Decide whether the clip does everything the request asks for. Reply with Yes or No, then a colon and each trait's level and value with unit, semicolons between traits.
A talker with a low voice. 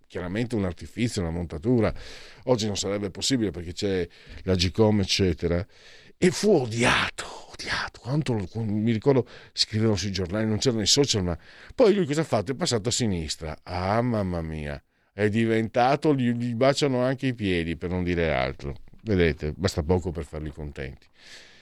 Yes: low, 105 Hz